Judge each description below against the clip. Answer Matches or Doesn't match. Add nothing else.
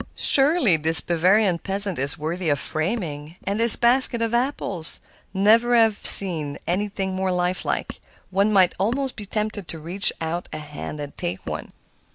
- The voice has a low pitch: Doesn't match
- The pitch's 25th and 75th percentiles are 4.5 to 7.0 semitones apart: Matches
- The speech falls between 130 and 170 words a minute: Matches